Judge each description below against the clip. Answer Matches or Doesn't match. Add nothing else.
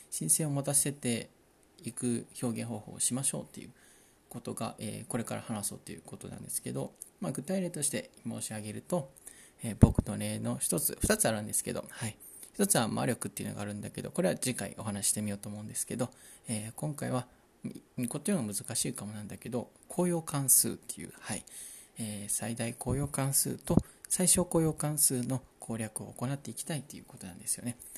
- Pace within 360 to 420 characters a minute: Matches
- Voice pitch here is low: Matches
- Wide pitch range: Doesn't match